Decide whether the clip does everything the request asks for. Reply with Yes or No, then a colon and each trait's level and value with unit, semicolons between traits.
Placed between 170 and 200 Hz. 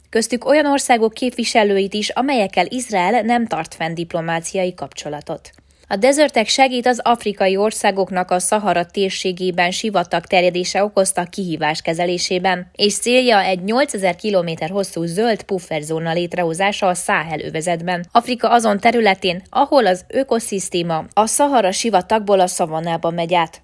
Yes: high, 190 Hz